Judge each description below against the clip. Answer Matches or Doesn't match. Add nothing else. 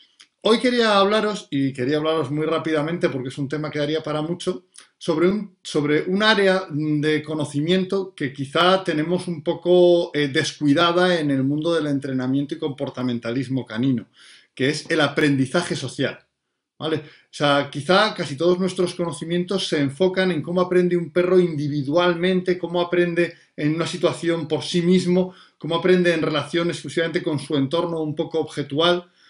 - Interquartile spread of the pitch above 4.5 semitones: Doesn't match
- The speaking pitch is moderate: Matches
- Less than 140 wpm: Doesn't match